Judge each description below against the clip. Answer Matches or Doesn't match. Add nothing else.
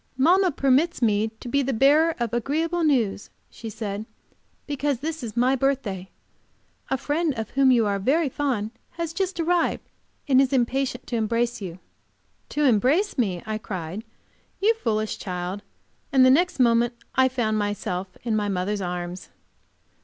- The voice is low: Doesn't match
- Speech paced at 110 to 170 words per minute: Matches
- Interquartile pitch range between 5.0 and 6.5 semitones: Matches